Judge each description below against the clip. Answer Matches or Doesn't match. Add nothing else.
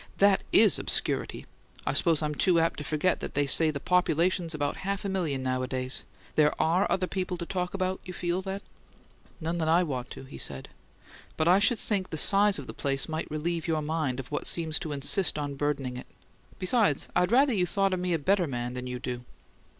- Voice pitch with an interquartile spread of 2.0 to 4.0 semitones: Doesn't match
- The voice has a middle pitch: Matches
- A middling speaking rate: Doesn't match